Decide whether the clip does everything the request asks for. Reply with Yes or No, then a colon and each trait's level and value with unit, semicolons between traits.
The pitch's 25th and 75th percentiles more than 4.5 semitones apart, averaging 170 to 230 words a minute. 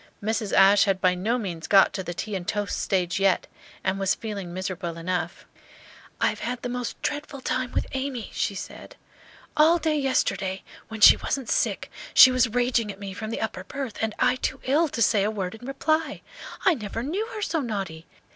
Yes: average, 5.1 semitones; fast, 205 wpm